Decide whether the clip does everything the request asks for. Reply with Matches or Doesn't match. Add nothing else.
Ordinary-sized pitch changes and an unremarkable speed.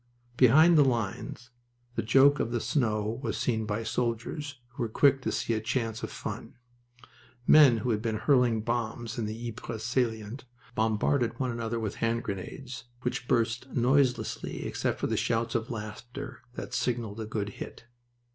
Doesn't match